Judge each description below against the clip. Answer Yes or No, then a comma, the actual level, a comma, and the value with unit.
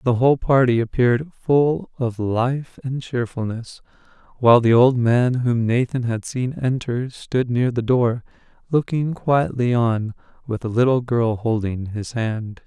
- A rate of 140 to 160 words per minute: Yes, average, 150 wpm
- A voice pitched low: Yes, low, 120 Hz